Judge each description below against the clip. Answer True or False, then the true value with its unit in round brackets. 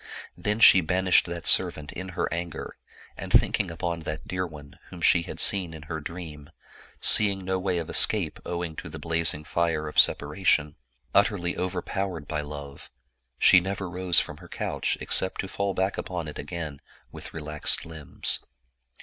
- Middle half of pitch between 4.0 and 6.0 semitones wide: False (3.2 semitones)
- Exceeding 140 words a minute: True (165 wpm)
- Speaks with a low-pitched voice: True (85 Hz)